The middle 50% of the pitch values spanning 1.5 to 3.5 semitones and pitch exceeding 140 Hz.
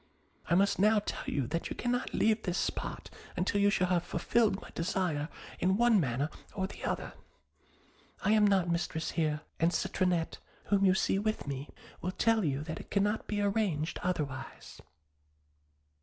No: average, 4.1 semitones; medium, 185 Hz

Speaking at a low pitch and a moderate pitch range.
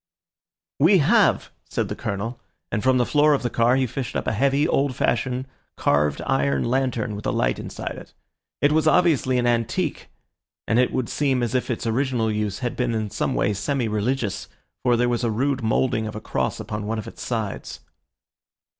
Yes: low, 120 Hz; average, 3.6 semitones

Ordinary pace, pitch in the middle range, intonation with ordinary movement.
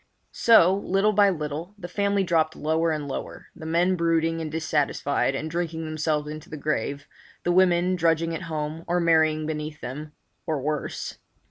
No: average, 160 wpm; medium, 160 Hz; narrow, 2.3 semitones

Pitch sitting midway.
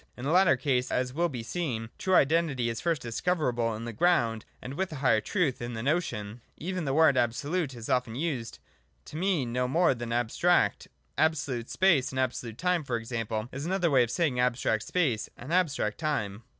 No: low, 130 Hz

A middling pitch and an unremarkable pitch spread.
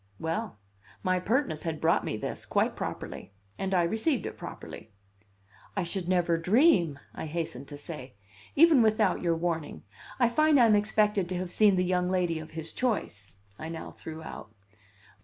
Yes: medium, 180 Hz; average, 4.7 semitones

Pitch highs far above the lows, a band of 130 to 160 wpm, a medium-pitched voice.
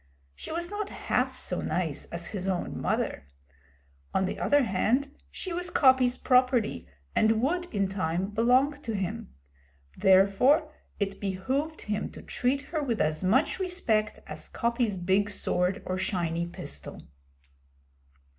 No: wide, 6.6 semitones; average, 140 wpm; high, 220 Hz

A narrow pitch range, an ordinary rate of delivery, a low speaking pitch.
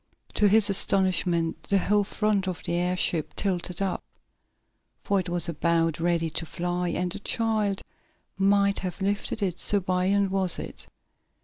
No: narrow, 2.3 semitones; average, 150 wpm; medium, 185 Hz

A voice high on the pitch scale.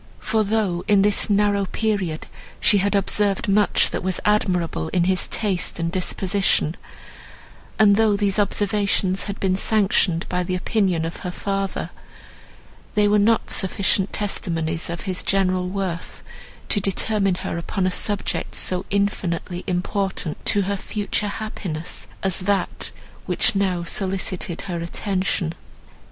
Yes: high, 195 Hz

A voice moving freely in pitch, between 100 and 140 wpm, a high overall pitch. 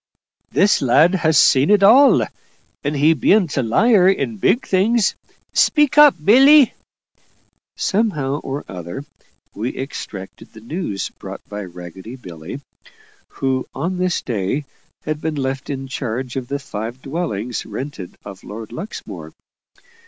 No: wide, 8.5 semitones; slow, 135 wpm; medium, 140 Hz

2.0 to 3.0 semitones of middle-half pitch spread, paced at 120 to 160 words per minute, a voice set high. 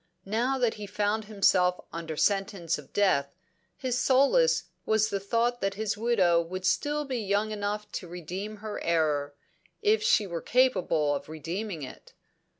No: average, 4.5 semitones; average, 155 wpm; high, 205 Hz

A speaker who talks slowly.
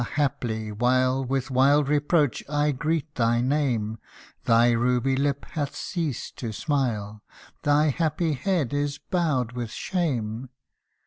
Yes: slow, 125 wpm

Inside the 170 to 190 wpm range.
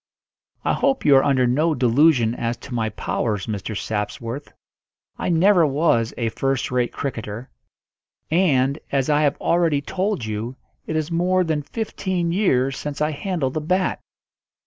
No: average, 155 wpm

